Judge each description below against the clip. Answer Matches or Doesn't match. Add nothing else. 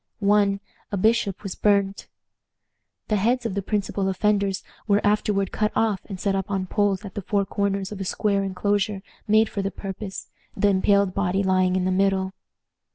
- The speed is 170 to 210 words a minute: Matches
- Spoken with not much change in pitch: Matches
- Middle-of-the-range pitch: Doesn't match